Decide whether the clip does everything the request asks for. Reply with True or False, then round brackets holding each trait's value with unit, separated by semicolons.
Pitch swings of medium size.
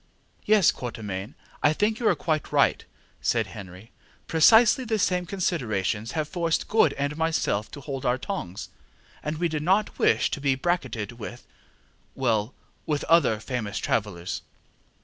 False (8.0 semitones)